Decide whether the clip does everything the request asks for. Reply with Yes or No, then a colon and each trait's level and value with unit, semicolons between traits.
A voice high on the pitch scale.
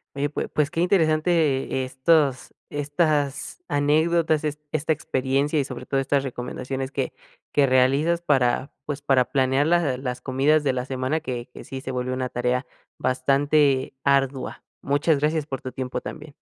No: medium, 140 Hz